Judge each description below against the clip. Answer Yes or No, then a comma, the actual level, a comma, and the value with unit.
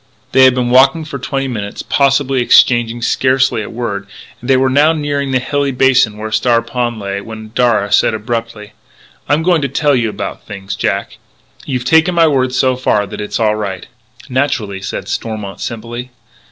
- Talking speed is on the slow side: No, average, 185 wpm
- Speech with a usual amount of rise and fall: Yes, average, 3.7 semitones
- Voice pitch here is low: Yes, low, 125 Hz